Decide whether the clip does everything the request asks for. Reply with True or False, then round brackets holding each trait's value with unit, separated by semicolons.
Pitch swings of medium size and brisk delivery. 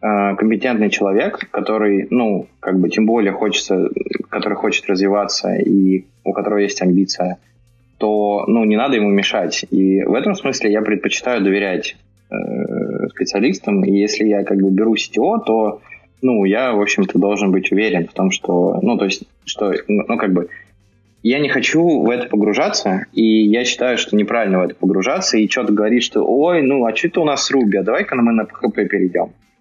False (2.2 semitones; 180 wpm)